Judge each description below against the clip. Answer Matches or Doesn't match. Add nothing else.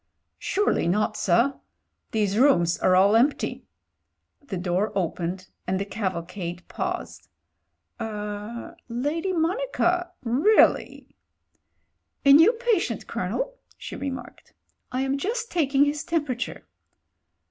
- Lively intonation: Matches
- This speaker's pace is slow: Matches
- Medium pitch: Doesn't match